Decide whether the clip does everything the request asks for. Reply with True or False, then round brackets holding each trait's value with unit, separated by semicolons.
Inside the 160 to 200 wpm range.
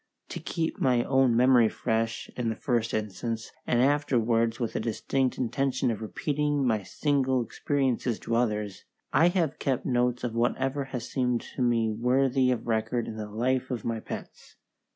True (170 wpm)